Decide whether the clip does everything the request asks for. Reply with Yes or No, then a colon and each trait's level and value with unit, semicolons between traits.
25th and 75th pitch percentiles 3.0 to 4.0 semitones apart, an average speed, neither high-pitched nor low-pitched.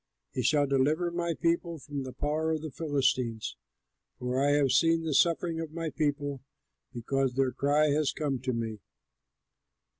Yes: average, 3.3 semitones; average, 160 wpm; medium, 145 Hz